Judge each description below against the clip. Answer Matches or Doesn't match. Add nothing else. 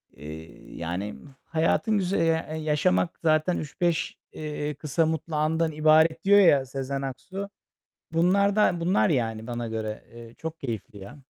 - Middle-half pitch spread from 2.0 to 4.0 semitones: Doesn't match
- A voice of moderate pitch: Matches